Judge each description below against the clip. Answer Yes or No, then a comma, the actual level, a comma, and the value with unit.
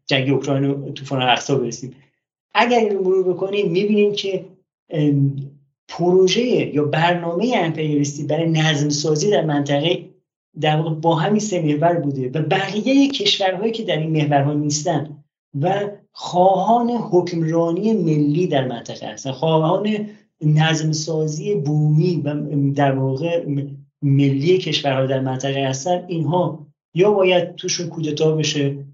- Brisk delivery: No, average, 125 wpm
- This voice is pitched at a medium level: Yes, medium, 160 Hz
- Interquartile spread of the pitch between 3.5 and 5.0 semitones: Yes, average, 4.2 semitones